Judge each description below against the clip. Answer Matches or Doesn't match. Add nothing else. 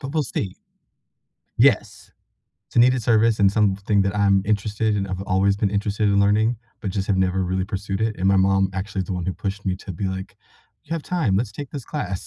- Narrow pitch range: Matches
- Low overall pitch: Matches